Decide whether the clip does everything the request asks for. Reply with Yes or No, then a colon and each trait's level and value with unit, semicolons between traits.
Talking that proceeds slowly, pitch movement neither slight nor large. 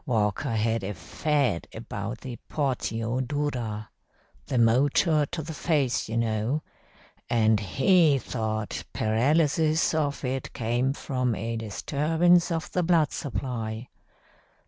Yes: slow, 120 wpm; average, 5.0 semitones